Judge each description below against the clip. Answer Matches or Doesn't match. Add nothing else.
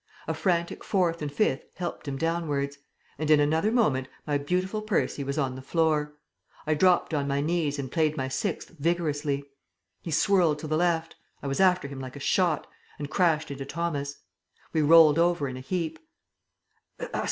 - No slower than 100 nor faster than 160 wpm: Doesn't match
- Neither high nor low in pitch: Matches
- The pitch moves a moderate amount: Matches